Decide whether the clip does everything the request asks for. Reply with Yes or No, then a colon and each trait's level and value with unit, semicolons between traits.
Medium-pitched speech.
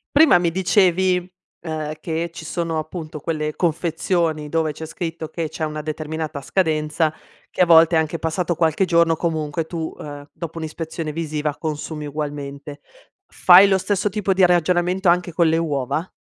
Yes: medium, 160 Hz